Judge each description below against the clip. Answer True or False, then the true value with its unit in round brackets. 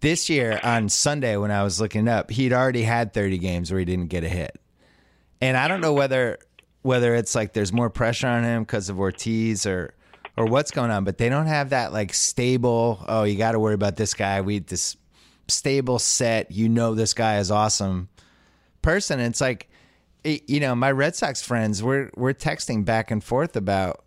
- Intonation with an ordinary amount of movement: True (3.8 semitones)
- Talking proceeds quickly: True (210 wpm)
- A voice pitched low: True (115 Hz)